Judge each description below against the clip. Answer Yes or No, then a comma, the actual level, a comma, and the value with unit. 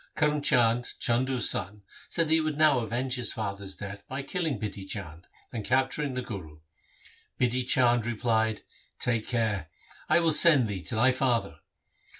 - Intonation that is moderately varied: Yes, average, 4.0 semitones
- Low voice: Yes, low, 120 Hz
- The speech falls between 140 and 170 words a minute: Yes, average, 165 wpm